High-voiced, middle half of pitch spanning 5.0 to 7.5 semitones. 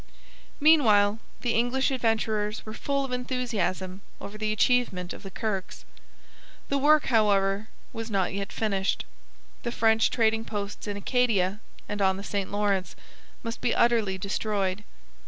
No: high, 215 Hz; average, 3.1 semitones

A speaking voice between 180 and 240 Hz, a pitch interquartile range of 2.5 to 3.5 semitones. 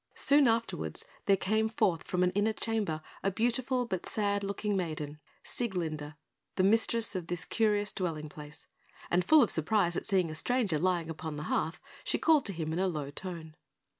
No: medium, 185 Hz; average, 5.3 semitones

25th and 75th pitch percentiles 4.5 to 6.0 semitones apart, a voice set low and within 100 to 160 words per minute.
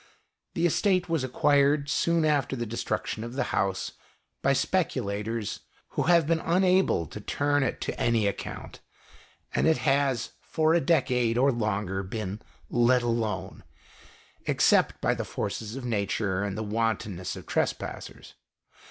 Yes: wide, 5.6 semitones; low, 120 Hz; average, 150 wpm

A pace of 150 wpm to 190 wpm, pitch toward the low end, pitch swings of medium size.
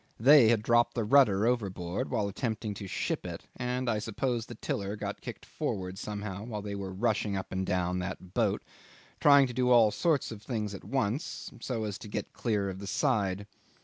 No: average, 200 wpm; low, 105 Hz; average, 3.6 semitones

